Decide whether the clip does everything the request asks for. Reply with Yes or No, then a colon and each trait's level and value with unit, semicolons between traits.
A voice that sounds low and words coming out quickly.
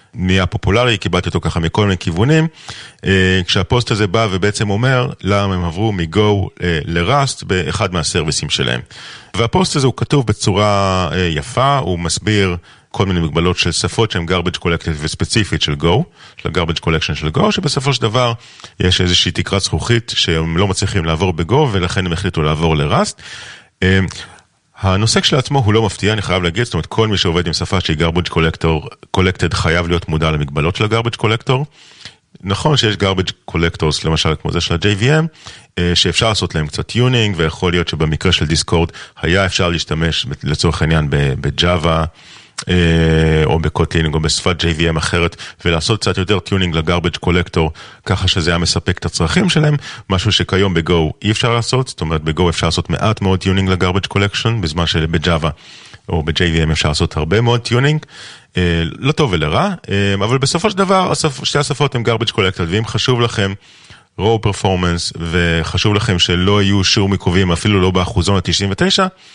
Yes: very low, 95 Hz; fast, 160 wpm